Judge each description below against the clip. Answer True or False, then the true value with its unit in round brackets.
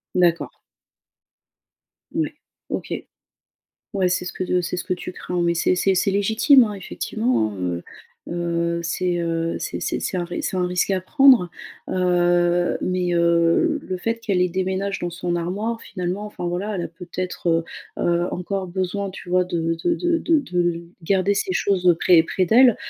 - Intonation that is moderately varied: False (2.3 semitones)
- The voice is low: False (180 Hz)